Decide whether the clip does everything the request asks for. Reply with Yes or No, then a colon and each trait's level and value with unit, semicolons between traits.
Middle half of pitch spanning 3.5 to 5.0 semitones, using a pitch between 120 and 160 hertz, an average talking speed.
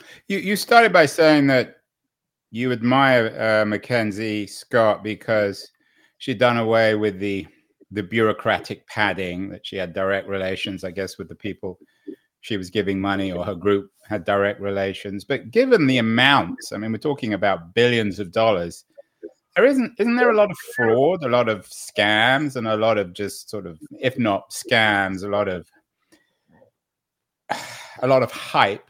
No: average, 4.1 semitones; low, 110 Hz; average, 170 wpm